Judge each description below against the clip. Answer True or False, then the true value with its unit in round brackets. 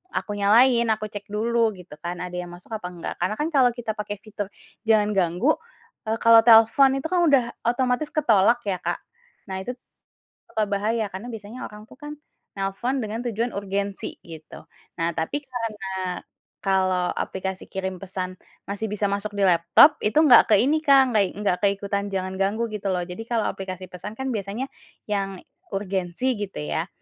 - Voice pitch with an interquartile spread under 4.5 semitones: True (3.6 semitones)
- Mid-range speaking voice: False (205 Hz)